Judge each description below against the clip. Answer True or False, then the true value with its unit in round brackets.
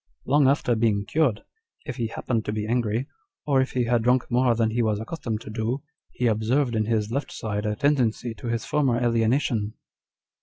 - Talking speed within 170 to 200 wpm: True (195 wpm)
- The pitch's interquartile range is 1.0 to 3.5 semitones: True (2.8 semitones)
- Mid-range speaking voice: False (115 Hz)